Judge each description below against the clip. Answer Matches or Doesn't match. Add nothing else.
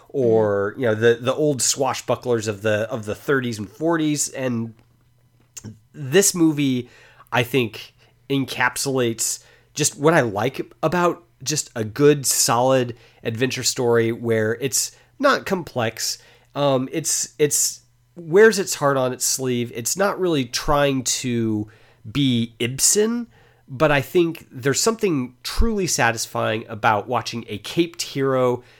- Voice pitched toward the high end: Doesn't match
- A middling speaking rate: Doesn't match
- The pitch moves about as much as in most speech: Matches